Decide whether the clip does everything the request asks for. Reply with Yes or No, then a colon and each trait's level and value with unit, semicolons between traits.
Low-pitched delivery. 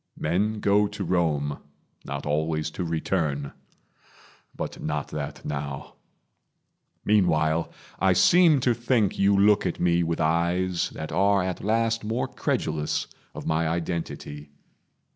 Yes: very low, 85 Hz